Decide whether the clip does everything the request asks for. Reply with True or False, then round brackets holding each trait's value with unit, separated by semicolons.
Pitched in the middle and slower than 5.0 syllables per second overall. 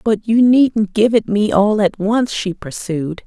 False (210 Hz; 3.8 syllables/s)